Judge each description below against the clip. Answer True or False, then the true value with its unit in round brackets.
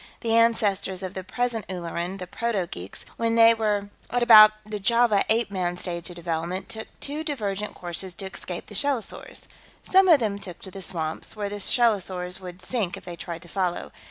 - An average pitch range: True (4.1 semitones)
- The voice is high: True (195 Hz)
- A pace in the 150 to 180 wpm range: False (195 wpm)